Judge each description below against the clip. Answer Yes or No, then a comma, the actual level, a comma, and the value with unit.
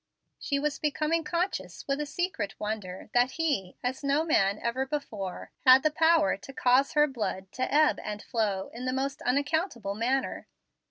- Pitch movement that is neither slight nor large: No, wide, 5.7 semitones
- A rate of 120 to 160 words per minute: No, average, 170 wpm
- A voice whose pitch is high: Yes, very high, 265 Hz